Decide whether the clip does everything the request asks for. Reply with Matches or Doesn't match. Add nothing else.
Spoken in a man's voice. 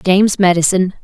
Doesn't match